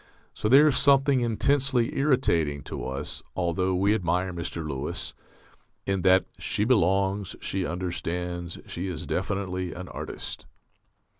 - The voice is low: Yes, very low, 95 Hz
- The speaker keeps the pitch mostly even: No, average, 4.1 semitones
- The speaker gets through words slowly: Yes, slow, 130 wpm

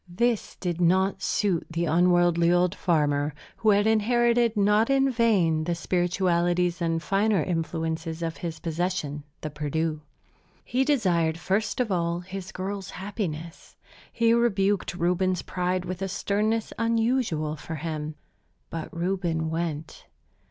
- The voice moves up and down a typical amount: Yes, average, 3.8 semitones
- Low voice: No, medium, 180 Hz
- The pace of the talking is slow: Yes, slow, 130 wpm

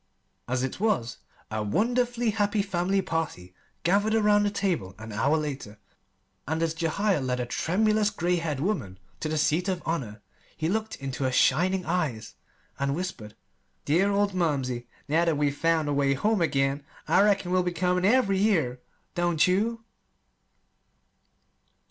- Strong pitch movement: Yes, wide, 6.4 semitones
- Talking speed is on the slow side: No, average, 155 wpm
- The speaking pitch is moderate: Yes, medium, 170 Hz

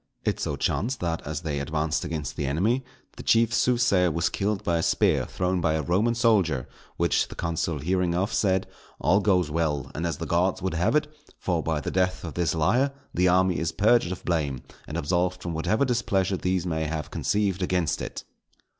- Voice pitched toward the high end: No, very low, 90 Hz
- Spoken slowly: No, average, 200 wpm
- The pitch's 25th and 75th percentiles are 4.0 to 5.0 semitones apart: No, average, 3.3 semitones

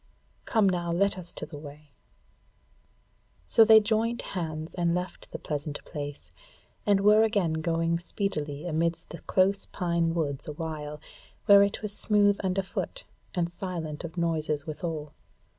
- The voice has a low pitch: No, medium, 170 Hz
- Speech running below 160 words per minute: Yes, average, 140 wpm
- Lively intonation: No, average, 4.2 semitones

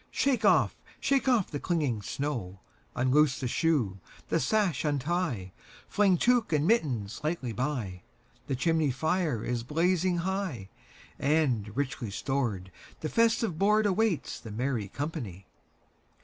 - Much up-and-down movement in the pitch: Yes, wide, 7.1 semitones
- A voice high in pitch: No, medium, 145 Hz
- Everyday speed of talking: No, slow, 110 wpm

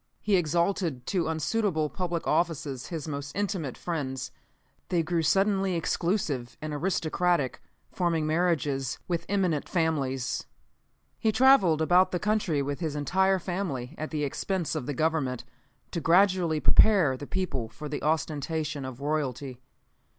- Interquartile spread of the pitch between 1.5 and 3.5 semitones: No, average, 4.0 semitones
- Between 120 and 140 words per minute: Yes, slow, 135 wpm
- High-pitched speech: No, medium, 160 Hz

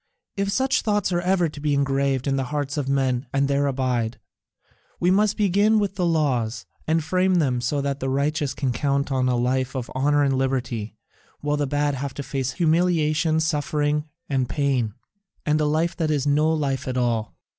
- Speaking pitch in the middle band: Yes, medium, 145 Hz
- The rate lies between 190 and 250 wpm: Yes, average, 195 wpm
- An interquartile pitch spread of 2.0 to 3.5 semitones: Yes, average, 3.1 semitones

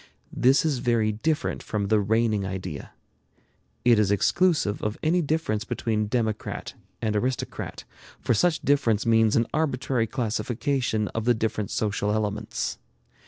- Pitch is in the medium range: No, low, 115 Hz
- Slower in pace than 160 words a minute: Yes, slow, 135 wpm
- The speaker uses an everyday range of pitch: Yes, average, 3.6 semitones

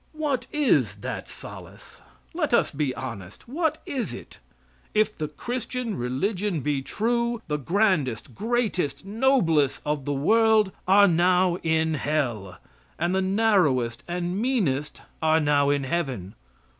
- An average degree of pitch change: No, wide, 7.6 semitones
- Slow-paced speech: Yes, slow, 130 wpm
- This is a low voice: No, medium, 175 Hz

